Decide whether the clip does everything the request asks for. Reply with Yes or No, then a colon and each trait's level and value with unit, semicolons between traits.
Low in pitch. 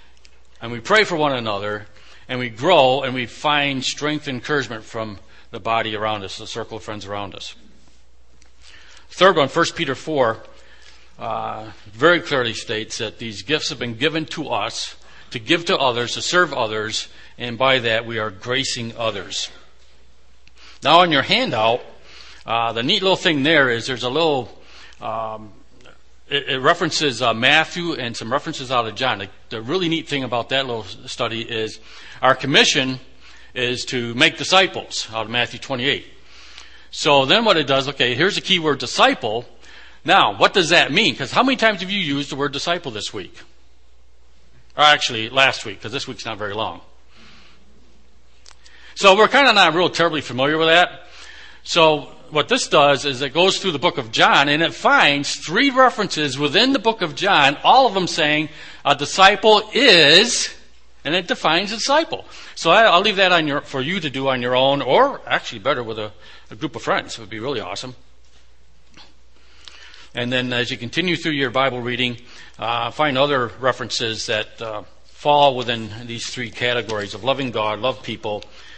Yes: low, 125 Hz